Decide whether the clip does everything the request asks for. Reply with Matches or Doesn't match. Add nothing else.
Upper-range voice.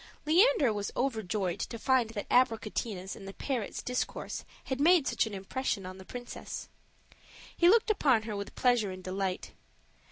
Matches